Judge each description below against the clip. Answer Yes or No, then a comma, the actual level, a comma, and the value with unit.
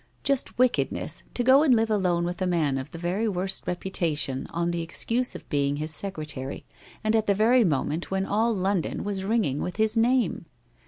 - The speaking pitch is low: No, high, 190 Hz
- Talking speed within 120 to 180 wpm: No, average, 195 wpm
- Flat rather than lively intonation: No, average, 5.2 semitones